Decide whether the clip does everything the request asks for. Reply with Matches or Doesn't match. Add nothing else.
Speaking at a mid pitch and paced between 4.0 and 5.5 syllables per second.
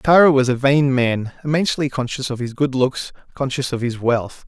Doesn't match